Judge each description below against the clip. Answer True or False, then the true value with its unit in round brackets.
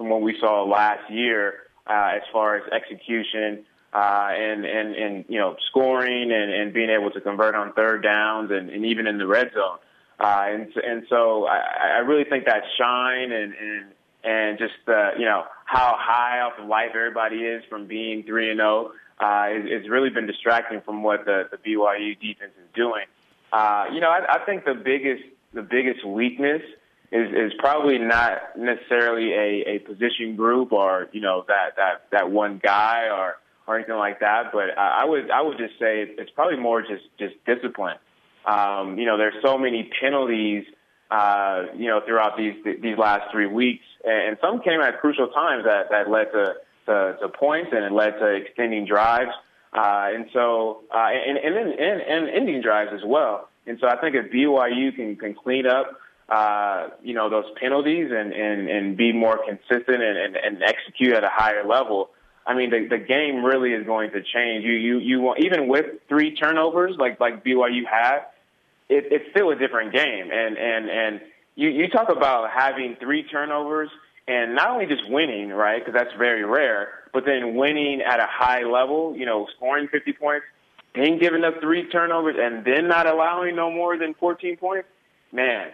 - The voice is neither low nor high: False (115 Hz)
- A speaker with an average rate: True (190 wpm)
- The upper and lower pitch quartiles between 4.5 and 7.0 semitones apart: False (3.8 semitones)